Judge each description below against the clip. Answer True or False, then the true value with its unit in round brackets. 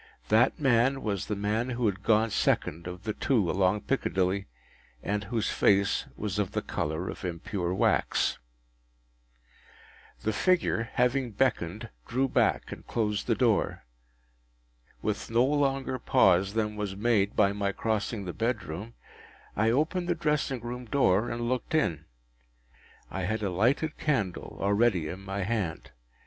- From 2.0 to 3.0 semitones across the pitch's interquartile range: False (4.1 semitones)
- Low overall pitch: True (110 Hz)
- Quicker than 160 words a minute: False (145 wpm)